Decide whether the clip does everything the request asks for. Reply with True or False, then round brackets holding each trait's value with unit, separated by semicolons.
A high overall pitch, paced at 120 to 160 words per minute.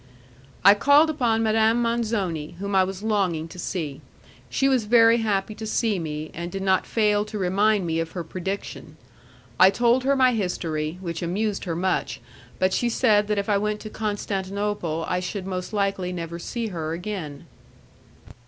False (200 Hz; 175 wpm)